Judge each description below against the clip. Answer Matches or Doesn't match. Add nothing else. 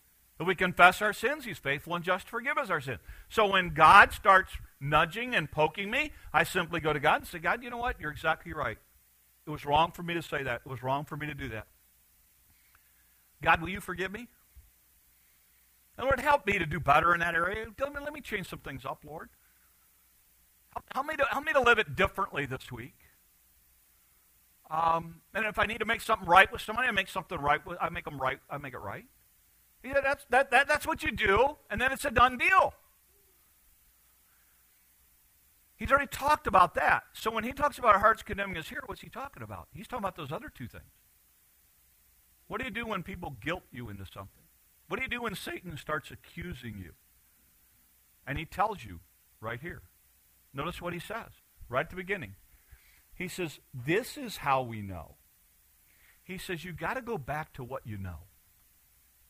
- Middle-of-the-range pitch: Matches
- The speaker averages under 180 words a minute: Doesn't match